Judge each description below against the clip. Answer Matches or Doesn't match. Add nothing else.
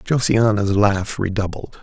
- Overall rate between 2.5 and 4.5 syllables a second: Matches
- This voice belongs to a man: Matches